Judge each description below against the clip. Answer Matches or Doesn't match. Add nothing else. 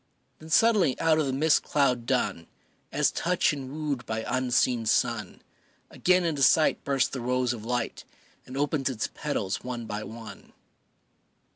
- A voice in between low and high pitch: Doesn't match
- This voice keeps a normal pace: Matches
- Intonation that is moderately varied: Matches